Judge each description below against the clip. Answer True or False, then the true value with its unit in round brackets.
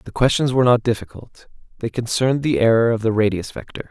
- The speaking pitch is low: True (120 Hz)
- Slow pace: False (200 wpm)